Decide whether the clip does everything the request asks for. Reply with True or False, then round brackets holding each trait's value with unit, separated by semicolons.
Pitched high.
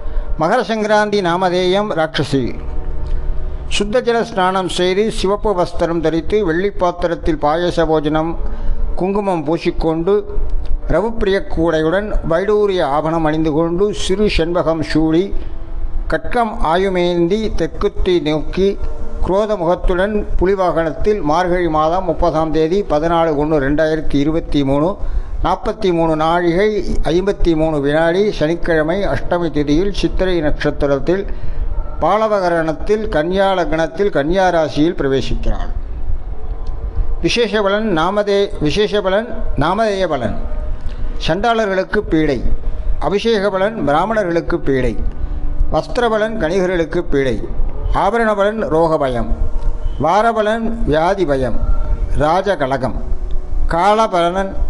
False (170 Hz)